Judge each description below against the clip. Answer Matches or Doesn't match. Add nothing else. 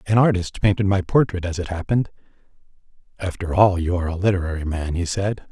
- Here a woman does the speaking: Doesn't match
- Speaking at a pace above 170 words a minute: Matches